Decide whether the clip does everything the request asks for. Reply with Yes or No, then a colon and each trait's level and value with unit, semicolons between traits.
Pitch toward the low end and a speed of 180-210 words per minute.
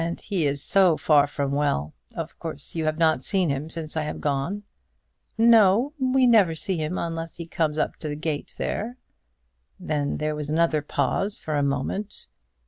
No: medium, 160 Hz; average, 190 wpm